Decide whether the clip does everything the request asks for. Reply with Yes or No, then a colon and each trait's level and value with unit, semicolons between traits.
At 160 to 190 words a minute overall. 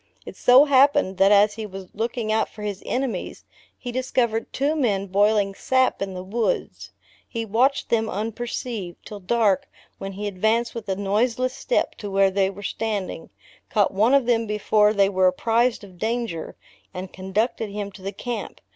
Yes: average, 175 wpm